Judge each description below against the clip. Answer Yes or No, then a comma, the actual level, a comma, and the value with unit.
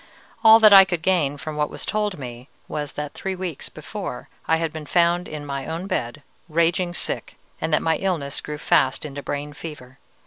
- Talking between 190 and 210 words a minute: Yes, average, 200 wpm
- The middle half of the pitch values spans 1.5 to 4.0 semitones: Yes, average, 3.7 semitones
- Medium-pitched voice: Yes, medium, 155 Hz